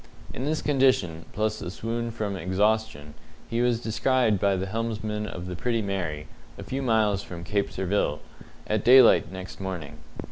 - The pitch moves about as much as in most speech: Yes, average, 3.8 semitones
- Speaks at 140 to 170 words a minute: Yes, average, 165 wpm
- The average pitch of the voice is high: No, low, 105 Hz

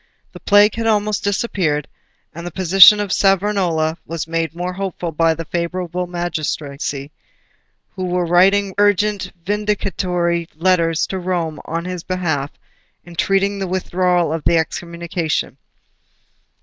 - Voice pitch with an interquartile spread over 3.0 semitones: No, average, 2.7 semitones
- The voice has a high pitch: No, medium, 175 Hz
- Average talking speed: No, slow, 125 wpm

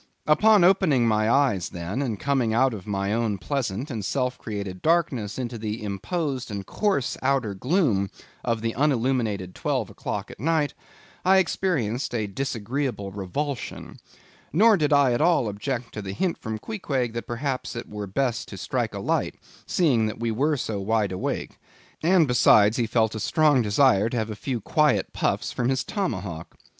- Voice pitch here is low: Yes, low, 120 Hz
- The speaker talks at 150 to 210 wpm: Yes, average, 175 wpm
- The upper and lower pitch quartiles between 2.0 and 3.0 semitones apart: No, average, 5.2 semitones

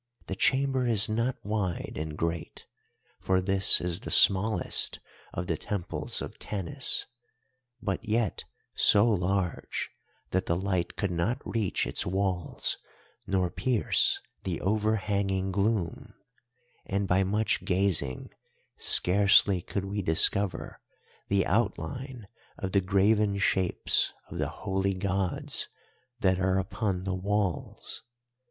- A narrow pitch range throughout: Yes, narrow, 2.3 semitones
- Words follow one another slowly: Yes, slow, 120 wpm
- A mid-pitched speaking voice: No, very low, 95 Hz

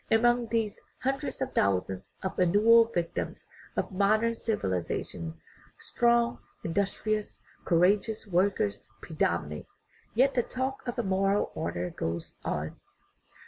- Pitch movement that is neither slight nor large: No, wide, 6.8 semitones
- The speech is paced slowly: Yes, slow, 115 wpm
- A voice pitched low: No, high, 200 Hz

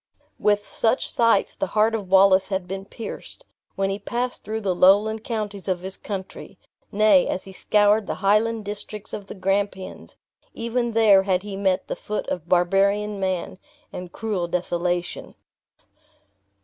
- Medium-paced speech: Yes, average, 155 wpm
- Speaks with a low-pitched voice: No, high, 200 Hz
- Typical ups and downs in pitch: No, narrow, 2.2 semitones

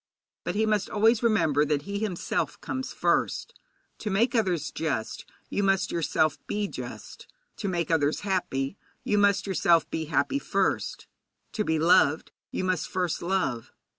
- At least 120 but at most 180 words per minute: Yes, average, 155 wpm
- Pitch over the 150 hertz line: Yes, medium, 185 Hz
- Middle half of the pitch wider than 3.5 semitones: Yes, average, 4.6 semitones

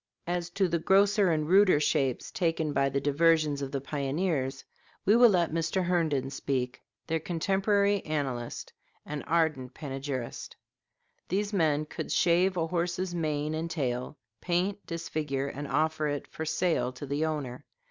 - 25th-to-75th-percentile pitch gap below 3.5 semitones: No, average, 3.8 semitones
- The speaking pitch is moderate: Yes, medium, 160 Hz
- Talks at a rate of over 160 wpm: No, average, 150 wpm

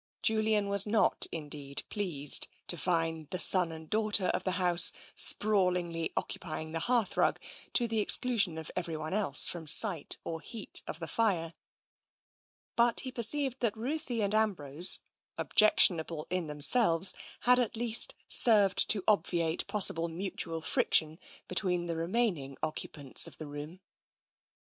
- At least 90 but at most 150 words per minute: Yes, average, 140 wpm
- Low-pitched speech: No, medium, 180 Hz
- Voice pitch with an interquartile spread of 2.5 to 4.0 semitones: No, average, 5.0 semitones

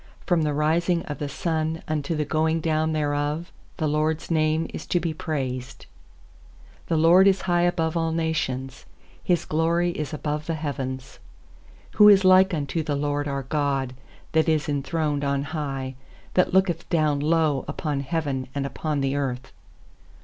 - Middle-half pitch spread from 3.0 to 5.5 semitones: No, narrow, 2.6 semitones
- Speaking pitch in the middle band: Yes, medium, 155 Hz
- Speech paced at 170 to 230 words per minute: No, average, 160 wpm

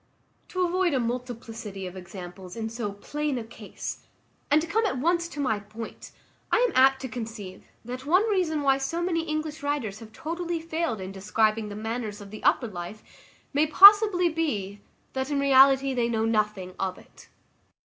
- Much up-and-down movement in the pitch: Yes, wide, 6.8 semitones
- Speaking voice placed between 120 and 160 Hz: No, very high, 250 Hz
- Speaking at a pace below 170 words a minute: No, average, 175 wpm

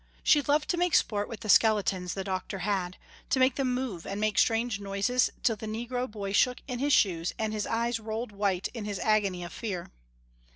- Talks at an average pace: No, fast, 210 wpm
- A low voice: No, high, 215 Hz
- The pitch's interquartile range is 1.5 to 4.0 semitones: Yes, average, 3.7 semitones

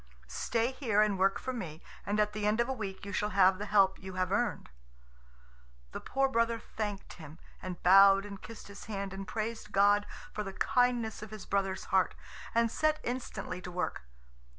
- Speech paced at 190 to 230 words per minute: Yes, average, 195 wpm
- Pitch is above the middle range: Yes, high, 205 Hz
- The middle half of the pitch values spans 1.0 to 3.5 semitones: Yes, average, 2.9 semitones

